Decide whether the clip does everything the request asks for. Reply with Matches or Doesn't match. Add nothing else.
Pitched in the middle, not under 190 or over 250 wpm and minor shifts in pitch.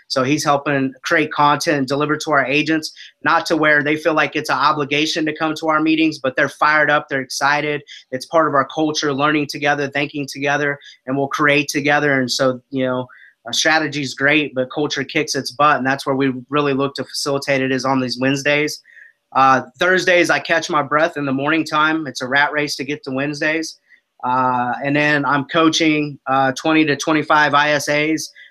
Matches